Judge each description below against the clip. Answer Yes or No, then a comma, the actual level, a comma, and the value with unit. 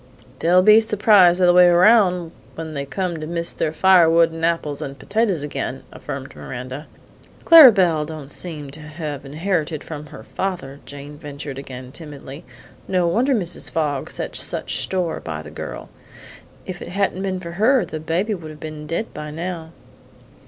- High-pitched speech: No, medium, 165 Hz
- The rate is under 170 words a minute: No, average, 175 wpm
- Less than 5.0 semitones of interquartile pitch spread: Yes, average, 3.8 semitones